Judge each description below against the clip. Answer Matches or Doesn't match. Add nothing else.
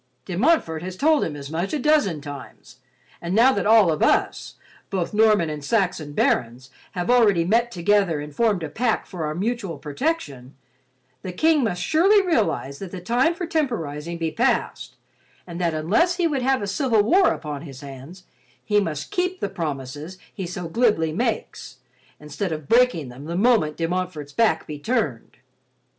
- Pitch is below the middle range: Doesn't match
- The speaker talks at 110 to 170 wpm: Doesn't match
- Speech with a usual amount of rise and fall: Doesn't match